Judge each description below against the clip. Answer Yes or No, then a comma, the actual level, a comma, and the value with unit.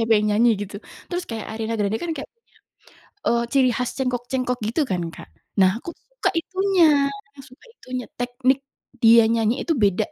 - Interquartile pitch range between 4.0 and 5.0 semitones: No, average, 3.4 semitones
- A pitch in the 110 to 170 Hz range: No, high, 245 Hz